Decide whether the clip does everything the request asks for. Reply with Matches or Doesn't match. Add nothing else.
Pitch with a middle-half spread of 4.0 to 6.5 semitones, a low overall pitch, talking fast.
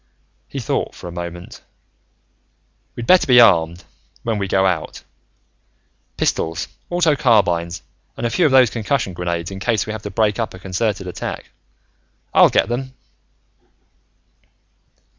Doesn't match